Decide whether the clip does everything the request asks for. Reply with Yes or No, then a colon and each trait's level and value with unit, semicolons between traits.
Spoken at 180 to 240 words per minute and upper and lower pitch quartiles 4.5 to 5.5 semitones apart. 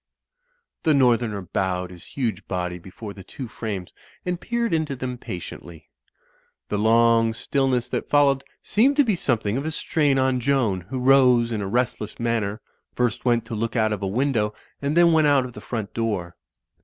Yes: average, 185 wpm; average, 4.8 semitones